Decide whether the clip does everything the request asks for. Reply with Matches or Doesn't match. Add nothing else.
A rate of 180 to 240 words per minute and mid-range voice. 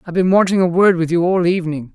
Doesn't match